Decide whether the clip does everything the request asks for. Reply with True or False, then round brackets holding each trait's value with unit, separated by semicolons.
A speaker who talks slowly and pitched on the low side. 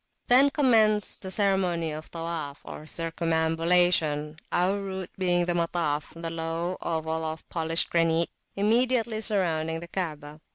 False (125 wpm; 170 Hz)